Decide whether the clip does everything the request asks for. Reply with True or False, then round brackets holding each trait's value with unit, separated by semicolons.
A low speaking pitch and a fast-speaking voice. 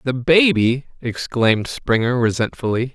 False (125 Hz; 100 wpm)